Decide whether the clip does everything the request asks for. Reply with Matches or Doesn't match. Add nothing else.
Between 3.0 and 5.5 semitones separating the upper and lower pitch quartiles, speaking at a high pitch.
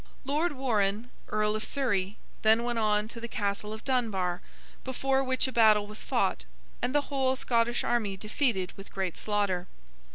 Matches